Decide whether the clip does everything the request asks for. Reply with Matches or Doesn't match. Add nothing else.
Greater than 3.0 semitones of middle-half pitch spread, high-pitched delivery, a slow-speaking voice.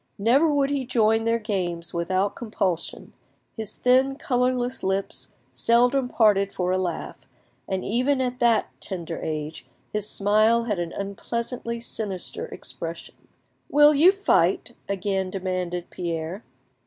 Matches